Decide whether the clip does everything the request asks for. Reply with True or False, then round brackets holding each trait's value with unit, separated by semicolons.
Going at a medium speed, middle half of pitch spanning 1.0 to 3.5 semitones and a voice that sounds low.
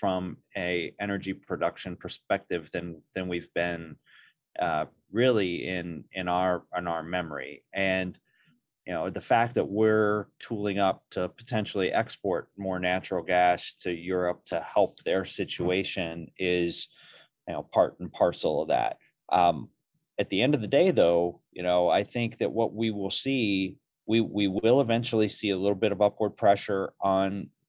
True (165 wpm; 2.6 semitones; 95 Hz)